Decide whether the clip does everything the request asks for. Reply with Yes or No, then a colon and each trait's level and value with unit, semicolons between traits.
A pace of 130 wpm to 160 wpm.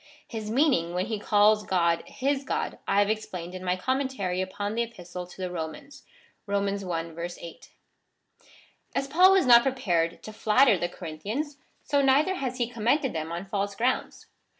No: average, 170 wpm